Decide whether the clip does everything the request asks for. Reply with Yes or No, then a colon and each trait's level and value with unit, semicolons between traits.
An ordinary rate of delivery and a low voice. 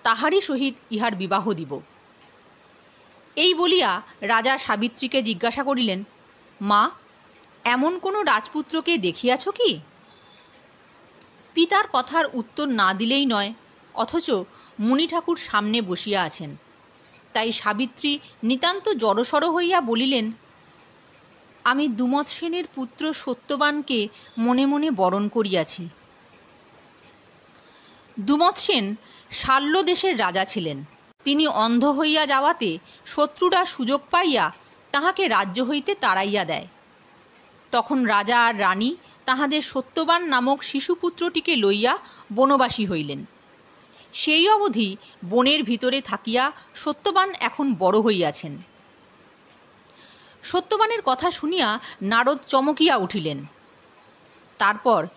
No: average, 95 wpm; very high, 260 Hz